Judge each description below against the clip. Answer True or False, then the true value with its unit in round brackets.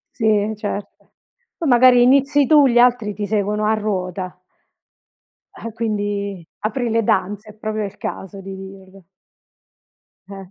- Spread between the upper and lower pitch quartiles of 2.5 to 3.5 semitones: True (2.9 semitones)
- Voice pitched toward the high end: True (210 Hz)